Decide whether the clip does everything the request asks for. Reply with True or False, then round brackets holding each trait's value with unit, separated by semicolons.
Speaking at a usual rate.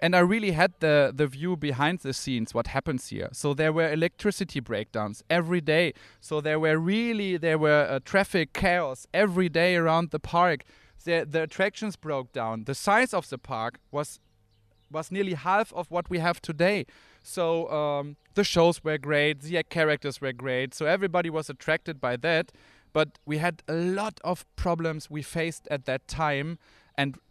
True (180 wpm)